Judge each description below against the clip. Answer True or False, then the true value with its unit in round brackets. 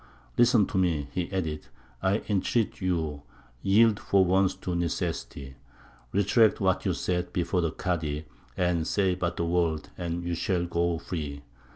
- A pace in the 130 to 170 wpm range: True (150 wpm)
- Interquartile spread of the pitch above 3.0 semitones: False (2.5 semitones)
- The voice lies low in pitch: True (90 Hz)